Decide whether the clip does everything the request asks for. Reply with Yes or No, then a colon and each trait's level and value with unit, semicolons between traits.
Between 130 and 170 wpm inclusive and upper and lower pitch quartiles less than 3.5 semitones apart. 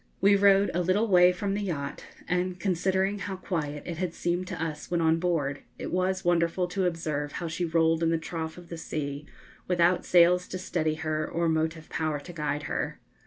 No: fast, 205 wpm; narrow, 2.4 semitones